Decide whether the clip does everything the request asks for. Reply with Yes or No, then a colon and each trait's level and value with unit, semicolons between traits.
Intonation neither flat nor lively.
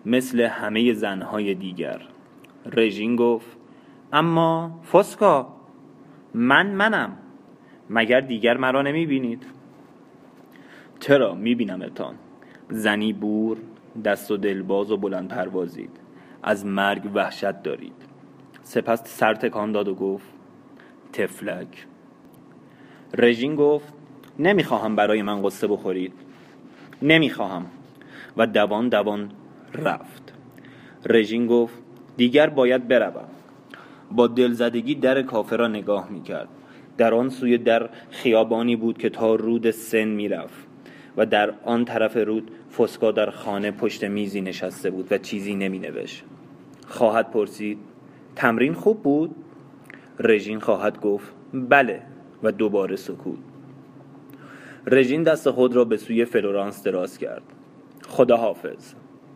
Yes: average, 4.1 semitones